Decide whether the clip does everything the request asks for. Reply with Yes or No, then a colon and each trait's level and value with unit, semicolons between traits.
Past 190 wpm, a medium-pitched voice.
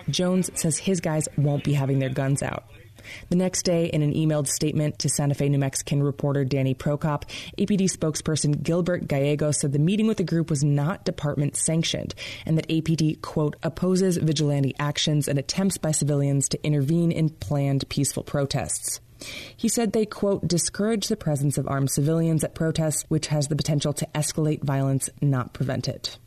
No: average, 180 wpm; medium, 150 Hz